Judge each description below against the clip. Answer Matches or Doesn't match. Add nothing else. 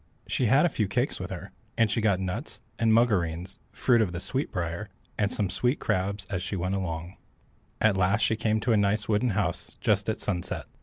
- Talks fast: Matches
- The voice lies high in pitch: Doesn't match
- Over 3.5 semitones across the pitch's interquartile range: Doesn't match